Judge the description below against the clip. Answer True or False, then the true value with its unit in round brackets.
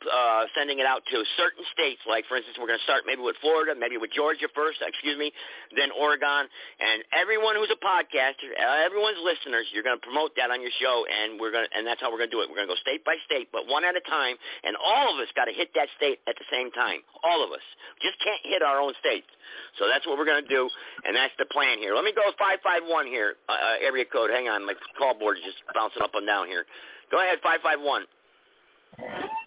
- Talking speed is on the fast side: True (250 wpm)